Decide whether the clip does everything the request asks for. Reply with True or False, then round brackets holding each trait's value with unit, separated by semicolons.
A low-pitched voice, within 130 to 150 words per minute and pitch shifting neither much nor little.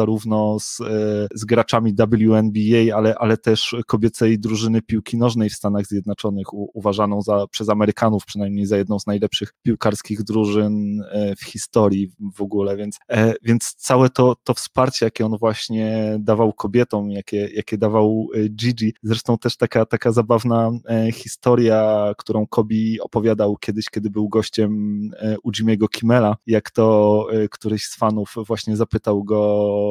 False (110 Hz; 140 wpm; 1.5 semitones)